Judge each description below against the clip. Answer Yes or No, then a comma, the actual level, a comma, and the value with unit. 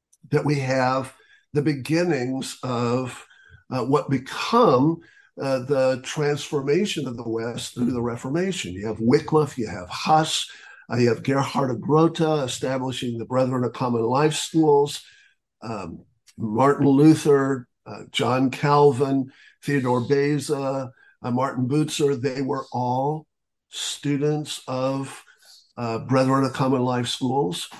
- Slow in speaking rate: Yes, slow, 125 wpm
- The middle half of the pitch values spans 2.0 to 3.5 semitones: Yes, average, 2.8 semitones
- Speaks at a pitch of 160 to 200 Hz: No, low, 135 Hz